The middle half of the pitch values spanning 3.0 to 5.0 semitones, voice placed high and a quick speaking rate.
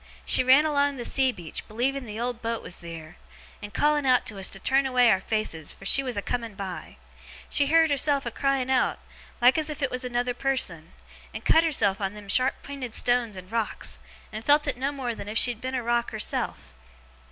Yes: average, 4.5 semitones; high, 245 Hz; fast, 220 wpm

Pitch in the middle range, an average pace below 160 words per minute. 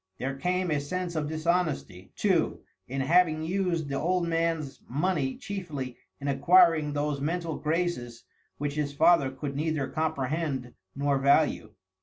Yes: medium, 155 Hz; average, 140 wpm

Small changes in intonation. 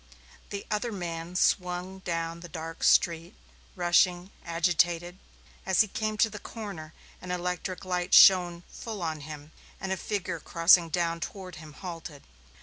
Yes: narrow, 2.1 semitones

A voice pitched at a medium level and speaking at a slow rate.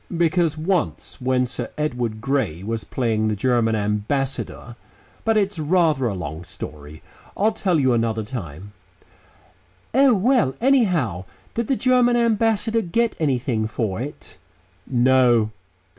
No: low, 130 Hz; slow, 130 wpm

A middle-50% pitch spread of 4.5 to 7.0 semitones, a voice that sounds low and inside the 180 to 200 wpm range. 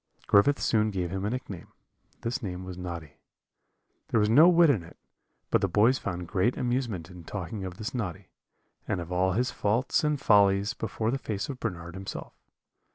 Yes: average, 4.9 semitones; low, 100 Hz; average, 185 wpm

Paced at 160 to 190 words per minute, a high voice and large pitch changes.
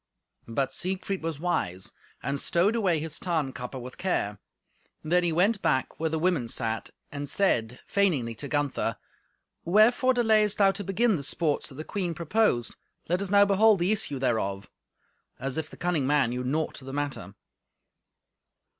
No: average, 165 wpm; medium, 160 Hz; wide, 6.6 semitones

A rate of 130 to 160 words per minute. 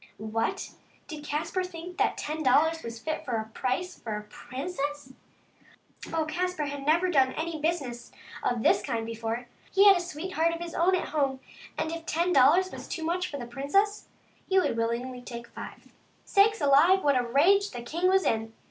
No: average, 190 wpm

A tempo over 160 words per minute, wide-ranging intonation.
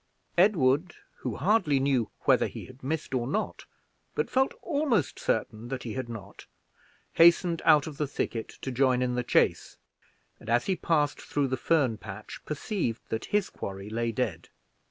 Yes: average, 170 wpm; wide, 5.7 semitones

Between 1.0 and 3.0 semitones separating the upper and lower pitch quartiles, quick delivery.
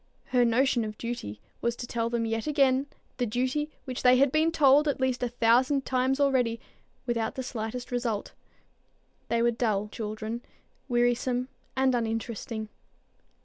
No: narrow, 2.4 semitones; average, 150 wpm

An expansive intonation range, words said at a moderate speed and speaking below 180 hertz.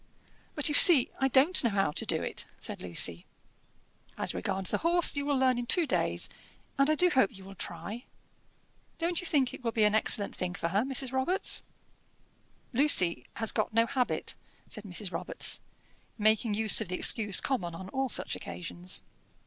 No: wide, 5.9 semitones; average, 185 wpm; high, 230 Hz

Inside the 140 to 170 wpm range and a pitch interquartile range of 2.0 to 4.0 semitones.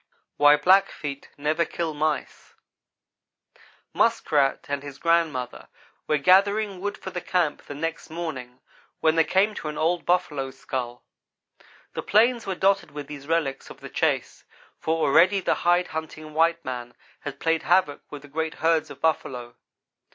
Yes: average, 155 wpm; average, 3.6 semitones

